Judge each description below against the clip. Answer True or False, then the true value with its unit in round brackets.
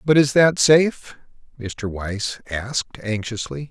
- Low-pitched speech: True (120 Hz)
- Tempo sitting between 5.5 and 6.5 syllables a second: False (3.9 syllables/s)